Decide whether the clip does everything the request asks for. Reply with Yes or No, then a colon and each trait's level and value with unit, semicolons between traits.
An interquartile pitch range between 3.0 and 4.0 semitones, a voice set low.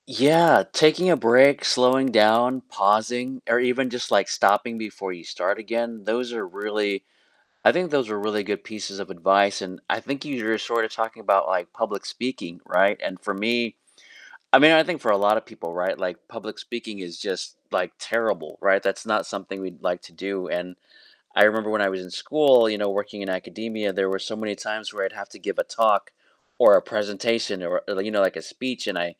Yes: average, 3.6 semitones; low, 110 Hz